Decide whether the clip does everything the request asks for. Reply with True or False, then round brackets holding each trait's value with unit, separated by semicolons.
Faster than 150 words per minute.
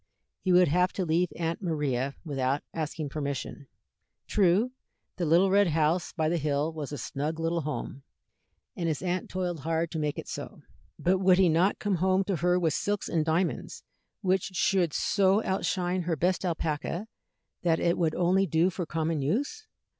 True (175 wpm)